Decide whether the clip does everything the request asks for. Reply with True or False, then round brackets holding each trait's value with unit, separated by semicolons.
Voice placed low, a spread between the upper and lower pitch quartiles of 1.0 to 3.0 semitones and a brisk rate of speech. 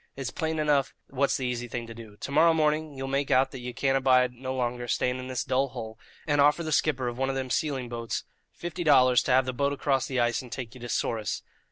True (130 Hz; 2.4 semitones; 255 wpm)